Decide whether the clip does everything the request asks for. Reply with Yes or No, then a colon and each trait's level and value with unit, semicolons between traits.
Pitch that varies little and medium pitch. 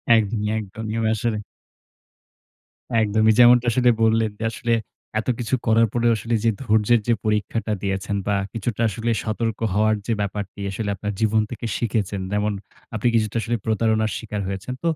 No: narrow, 1.8 semitones; low, 110 Hz